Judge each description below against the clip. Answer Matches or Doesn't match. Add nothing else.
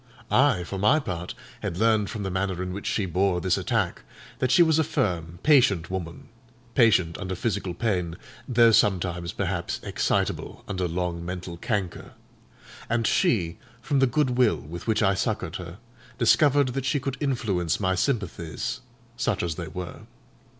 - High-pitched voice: Doesn't match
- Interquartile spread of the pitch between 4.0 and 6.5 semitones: Matches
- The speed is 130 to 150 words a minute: Doesn't match